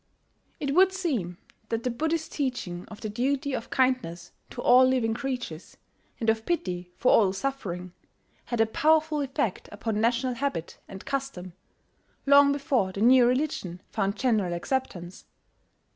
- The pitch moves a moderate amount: No, wide, 6.0 semitones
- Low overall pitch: No, high, 240 Hz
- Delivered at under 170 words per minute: Yes, average, 145 wpm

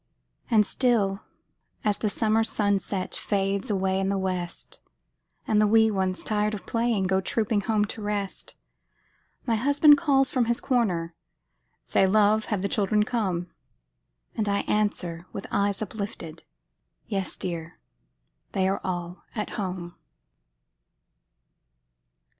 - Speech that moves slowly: Yes, slow, 130 wpm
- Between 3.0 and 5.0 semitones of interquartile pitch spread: No, narrow, 2.5 semitones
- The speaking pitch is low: No, high, 205 Hz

